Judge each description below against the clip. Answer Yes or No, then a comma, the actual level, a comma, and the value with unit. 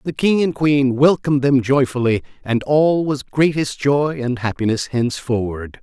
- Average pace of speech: Yes, average, 155 wpm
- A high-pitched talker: No, low, 135 Hz